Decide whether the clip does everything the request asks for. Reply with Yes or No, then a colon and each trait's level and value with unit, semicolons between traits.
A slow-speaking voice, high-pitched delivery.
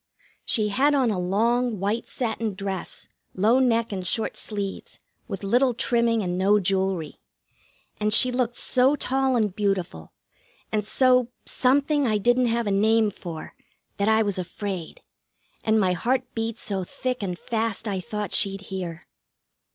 No: average, 155 wpm; high, 215 Hz